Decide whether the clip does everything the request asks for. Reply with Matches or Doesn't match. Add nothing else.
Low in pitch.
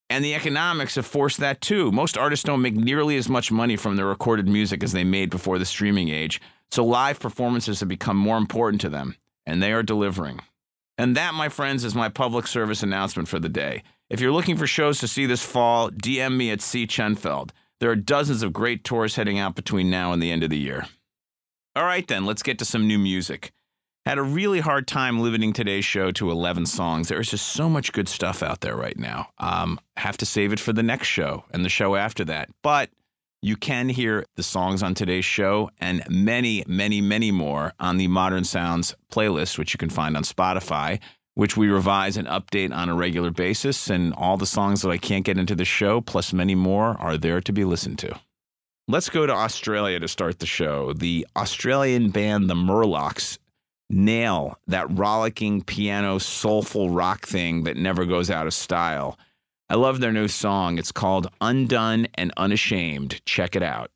Matches